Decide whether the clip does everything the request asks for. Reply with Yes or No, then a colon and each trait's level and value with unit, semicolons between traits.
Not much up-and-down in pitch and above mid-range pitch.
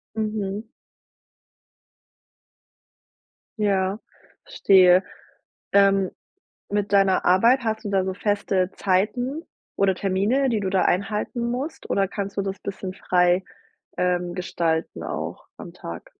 Yes: narrow, 2.2 semitones; high, 195 Hz